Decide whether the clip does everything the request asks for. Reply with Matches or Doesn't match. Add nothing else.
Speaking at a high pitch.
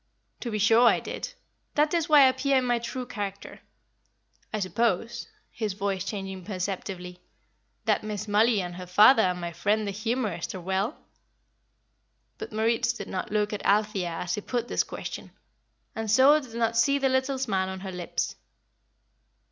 Matches